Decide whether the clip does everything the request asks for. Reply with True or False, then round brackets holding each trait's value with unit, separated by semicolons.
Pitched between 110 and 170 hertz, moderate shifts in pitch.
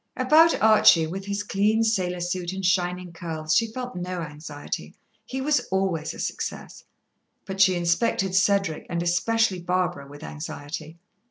False (180 Hz; 3.2 semitones)